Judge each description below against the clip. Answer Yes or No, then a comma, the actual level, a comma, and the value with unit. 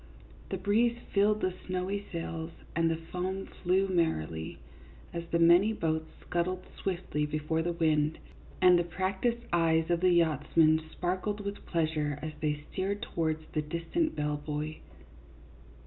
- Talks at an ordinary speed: Yes, average, 150 wpm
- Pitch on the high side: No, medium, 170 Hz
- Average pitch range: Yes, average, 3.0 semitones